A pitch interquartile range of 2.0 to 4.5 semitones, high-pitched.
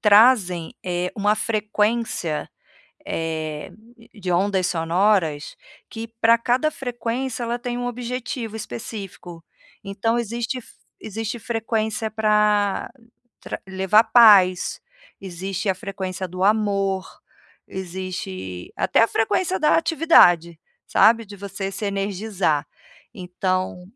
Yes: average, 3.8 semitones; high, 205 Hz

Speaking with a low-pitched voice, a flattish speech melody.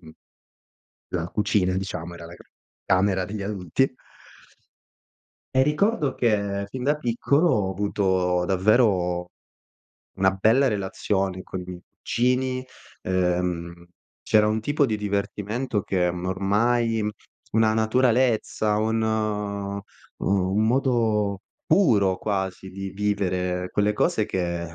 No: low, 100 Hz; average, 3.2 semitones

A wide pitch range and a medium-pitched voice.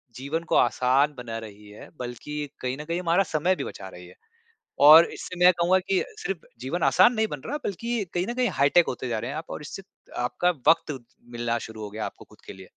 Yes: wide, 6.7 semitones; medium, 150 Hz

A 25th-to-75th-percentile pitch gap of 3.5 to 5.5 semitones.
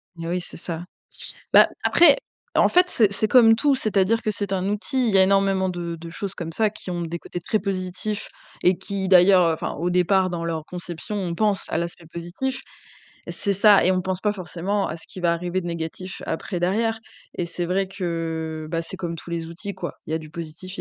No: average, 2.9 semitones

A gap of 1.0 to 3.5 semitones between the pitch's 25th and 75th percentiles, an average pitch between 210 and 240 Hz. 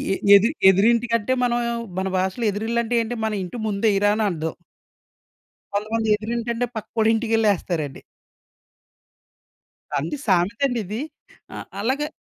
Yes: average, 2.7 semitones; high, 225 Hz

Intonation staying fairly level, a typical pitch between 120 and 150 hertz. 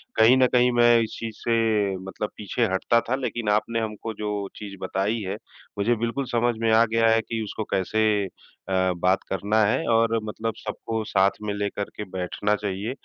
No: narrow, 2.1 semitones; low, 110 Hz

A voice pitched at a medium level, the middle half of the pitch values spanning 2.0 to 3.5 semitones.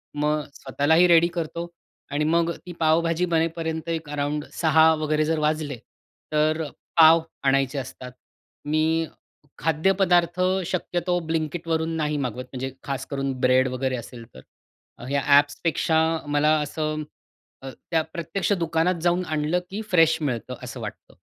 Yes: medium, 155 Hz; narrow, 2.4 semitones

